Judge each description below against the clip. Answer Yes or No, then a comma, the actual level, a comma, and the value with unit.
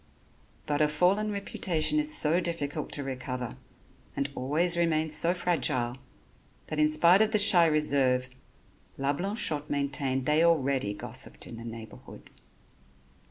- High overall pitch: No, medium, 150 Hz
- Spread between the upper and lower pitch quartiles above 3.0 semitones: Yes, average, 4.0 semitones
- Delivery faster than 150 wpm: No, slow, 135 wpm